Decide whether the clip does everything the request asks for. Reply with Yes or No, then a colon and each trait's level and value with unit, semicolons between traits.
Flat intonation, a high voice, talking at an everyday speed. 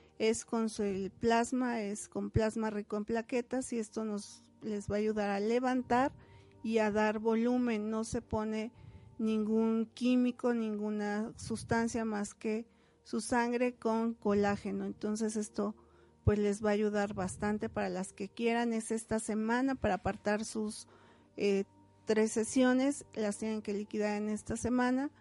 Yes: narrow, 1.8 semitones; high, 220 Hz; average, 155 wpm